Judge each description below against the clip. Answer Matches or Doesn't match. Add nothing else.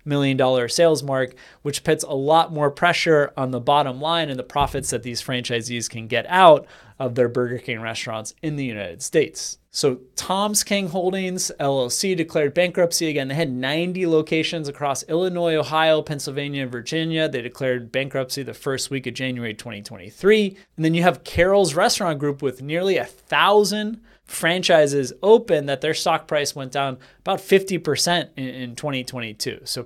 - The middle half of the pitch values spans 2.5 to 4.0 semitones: Doesn't match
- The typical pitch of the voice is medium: Matches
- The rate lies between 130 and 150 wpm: Doesn't match